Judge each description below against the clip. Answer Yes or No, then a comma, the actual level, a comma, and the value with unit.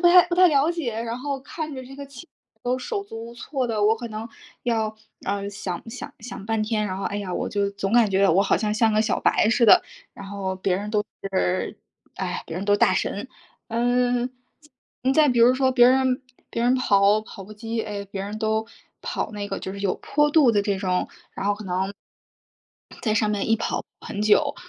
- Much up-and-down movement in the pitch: No, average, 3.7 semitones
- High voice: Yes, high, 220 Hz